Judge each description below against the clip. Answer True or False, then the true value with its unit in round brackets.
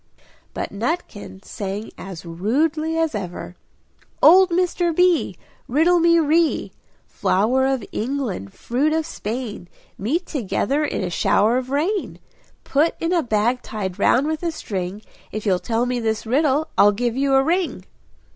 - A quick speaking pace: False (150 wpm)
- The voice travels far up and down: True (7.3 semitones)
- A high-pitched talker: True (260 Hz)